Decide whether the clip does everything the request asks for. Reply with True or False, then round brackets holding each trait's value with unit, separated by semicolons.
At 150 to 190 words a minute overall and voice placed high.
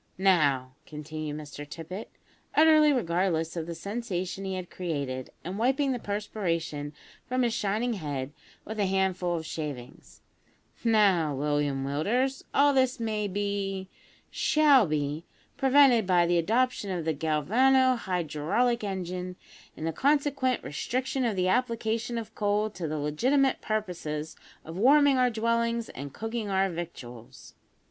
False (140 wpm; 195 Hz)